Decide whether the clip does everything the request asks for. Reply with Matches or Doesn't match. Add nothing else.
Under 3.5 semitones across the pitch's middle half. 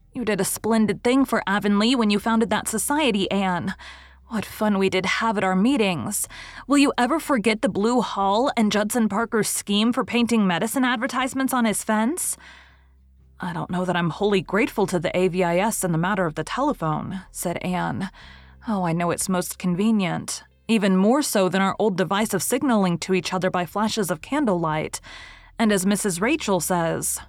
Doesn't match